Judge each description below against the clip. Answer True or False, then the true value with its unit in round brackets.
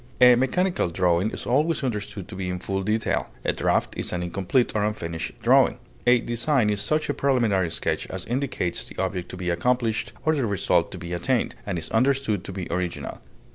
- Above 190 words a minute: True (200 wpm)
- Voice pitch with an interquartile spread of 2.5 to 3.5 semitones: False (5.5 semitones)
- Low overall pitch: True (105 Hz)